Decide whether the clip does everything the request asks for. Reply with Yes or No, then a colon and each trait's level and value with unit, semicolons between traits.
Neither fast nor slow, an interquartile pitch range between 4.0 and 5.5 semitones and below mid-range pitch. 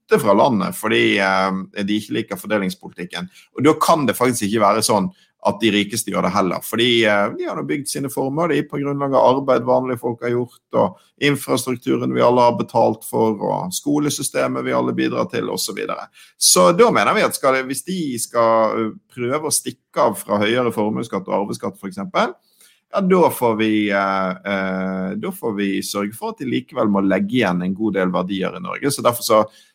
No: fast, 220 wpm; average, 4.3 semitones; low, 110 Hz